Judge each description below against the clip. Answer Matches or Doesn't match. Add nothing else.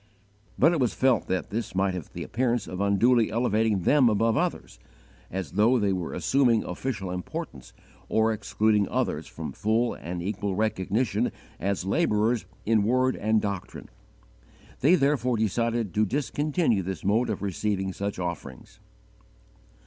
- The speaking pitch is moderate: Doesn't match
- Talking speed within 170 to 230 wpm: Doesn't match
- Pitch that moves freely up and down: Doesn't match